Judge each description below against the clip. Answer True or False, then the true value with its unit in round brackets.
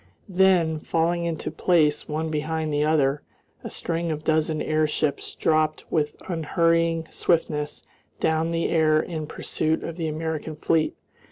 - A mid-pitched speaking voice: True (160 Hz)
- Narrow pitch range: True (1.3 semitones)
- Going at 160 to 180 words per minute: False (145 wpm)